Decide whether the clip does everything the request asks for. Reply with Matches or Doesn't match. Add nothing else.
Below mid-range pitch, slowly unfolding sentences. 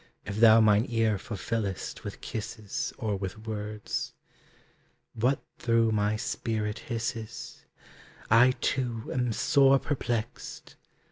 Matches